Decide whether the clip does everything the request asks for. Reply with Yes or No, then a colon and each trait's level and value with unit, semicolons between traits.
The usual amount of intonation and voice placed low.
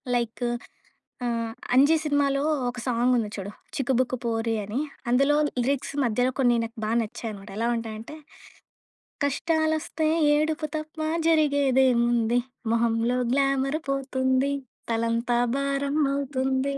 No: average, 3.2 semitones; very high, 260 Hz